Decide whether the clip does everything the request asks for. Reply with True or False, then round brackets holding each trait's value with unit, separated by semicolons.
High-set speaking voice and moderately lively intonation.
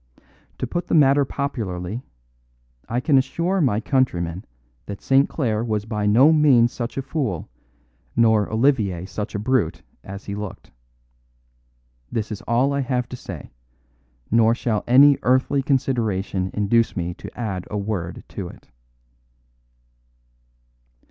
False (115 Hz; 4.6 semitones)